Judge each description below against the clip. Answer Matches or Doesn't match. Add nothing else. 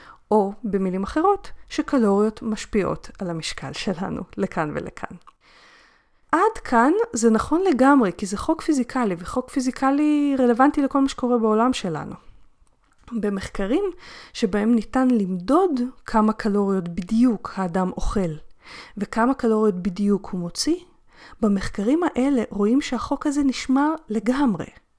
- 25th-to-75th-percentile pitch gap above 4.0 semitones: Matches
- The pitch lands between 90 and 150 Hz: Doesn't match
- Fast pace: Doesn't match